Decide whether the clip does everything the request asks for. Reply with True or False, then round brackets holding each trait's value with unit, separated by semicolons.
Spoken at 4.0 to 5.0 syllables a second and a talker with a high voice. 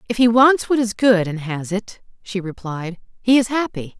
True (4.7 syllables/s; 210 Hz)